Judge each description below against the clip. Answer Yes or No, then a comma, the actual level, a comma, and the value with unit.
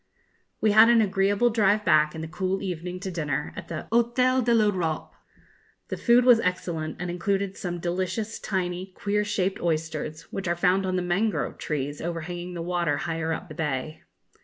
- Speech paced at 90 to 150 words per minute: No, average, 180 wpm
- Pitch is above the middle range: No, medium, 180 Hz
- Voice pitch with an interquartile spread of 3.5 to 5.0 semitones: Yes, average, 3.9 semitones